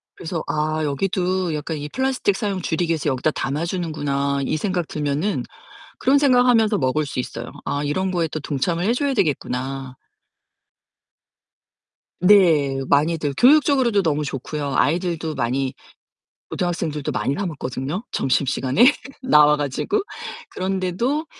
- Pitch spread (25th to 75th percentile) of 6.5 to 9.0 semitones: No, average, 5.2 semitones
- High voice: No, medium, 160 Hz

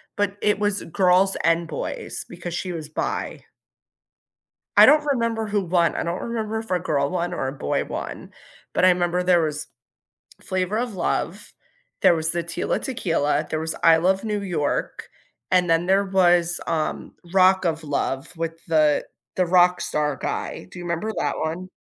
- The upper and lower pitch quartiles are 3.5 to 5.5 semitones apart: No, average, 2.7 semitones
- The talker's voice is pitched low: No, medium, 175 Hz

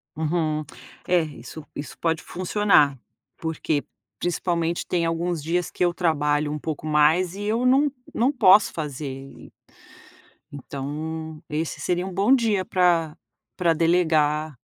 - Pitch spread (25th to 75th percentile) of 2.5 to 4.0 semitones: Yes, average, 3.0 semitones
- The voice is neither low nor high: Yes, medium, 165 Hz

